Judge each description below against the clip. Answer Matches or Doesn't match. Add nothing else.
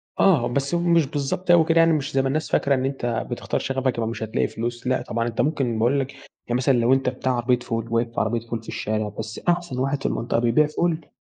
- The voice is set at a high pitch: Doesn't match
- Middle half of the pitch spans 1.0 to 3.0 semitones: Doesn't match